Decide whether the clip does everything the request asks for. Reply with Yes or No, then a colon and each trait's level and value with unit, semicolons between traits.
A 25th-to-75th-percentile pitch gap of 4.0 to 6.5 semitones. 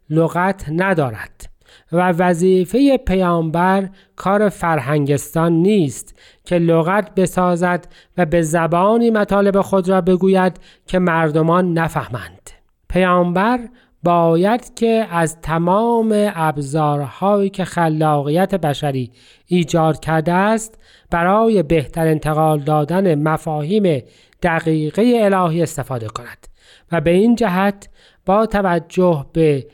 No: average, 3.5 semitones